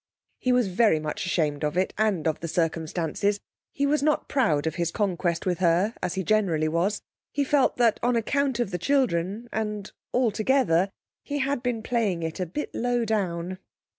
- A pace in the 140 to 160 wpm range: No, average, 185 wpm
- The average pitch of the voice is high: Yes, high, 200 Hz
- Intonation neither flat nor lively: No, wide, 6.1 semitones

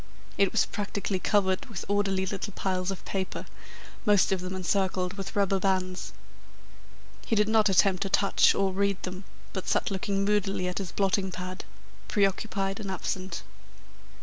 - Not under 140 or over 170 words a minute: Yes, average, 155 wpm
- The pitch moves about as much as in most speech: No, narrow, 1.3 semitones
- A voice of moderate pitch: No, high, 195 Hz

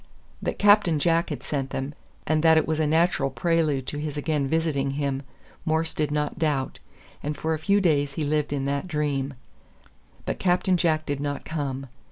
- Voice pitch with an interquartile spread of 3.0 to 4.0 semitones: No, narrow, 2.4 semitones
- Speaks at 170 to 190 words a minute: Yes, average, 185 wpm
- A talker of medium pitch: Yes, medium, 150 Hz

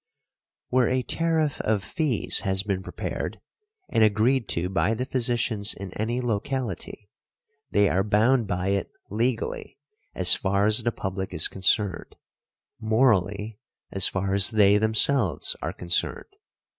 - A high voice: No, low, 105 Hz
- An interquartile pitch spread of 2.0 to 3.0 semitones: No, average, 3.7 semitones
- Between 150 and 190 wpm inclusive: No, slow, 135 wpm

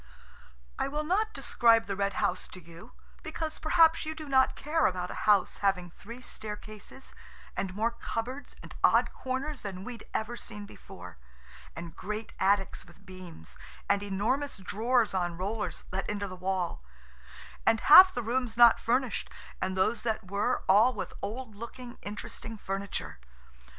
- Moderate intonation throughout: Yes, average, 4.8 semitones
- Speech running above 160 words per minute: No, average, 150 wpm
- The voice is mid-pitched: No, high, 210 Hz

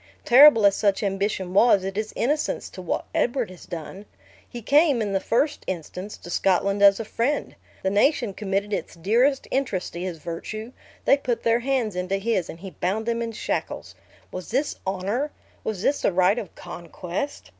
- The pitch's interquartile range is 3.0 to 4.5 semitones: Yes, average, 4.2 semitones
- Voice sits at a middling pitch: No, high, 205 Hz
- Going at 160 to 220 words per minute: Yes, average, 185 wpm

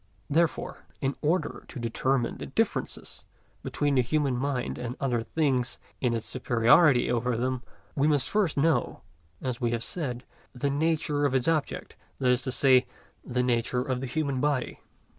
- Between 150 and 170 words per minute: Yes, average, 165 wpm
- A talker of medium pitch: No, low, 130 Hz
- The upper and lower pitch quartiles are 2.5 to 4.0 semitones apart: Yes, average, 2.8 semitones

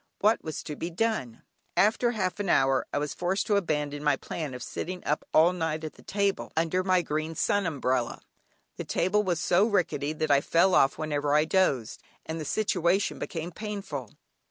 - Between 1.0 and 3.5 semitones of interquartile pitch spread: No, average, 4.4 semitones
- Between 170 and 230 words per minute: Yes, average, 190 wpm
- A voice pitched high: No, medium, 165 Hz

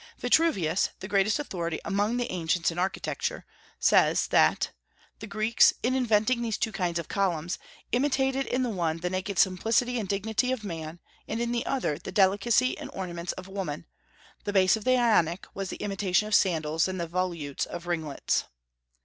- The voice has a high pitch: Yes, high, 195 Hz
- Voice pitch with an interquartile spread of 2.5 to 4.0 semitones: No, average, 4.7 semitones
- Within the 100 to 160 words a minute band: No, average, 175 wpm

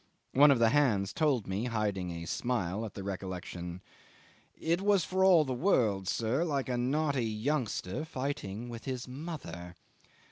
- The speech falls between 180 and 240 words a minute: No, average, 155 wpm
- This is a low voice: Yes, low, 120 Hz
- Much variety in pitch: Yes, wide, 6.9 semitones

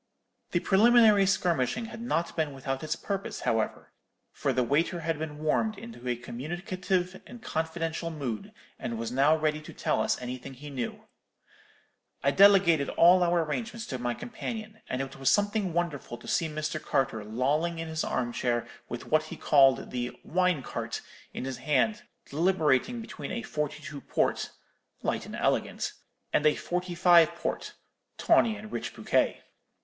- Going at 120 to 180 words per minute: Yes, average, 165 wpm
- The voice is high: No, medium, 160 Hz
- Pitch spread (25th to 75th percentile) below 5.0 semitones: No, wide, 5.6 semitones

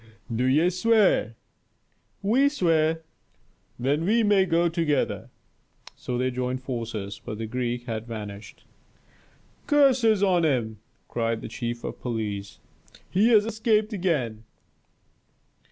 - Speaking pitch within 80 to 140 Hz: Yes, low, 135 Hz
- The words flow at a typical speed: No, slow, 120 wpm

